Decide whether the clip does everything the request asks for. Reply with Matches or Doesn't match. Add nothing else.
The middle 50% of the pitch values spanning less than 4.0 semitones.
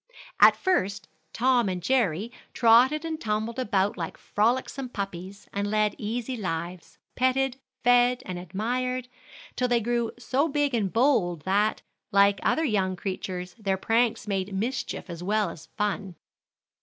Doesn't match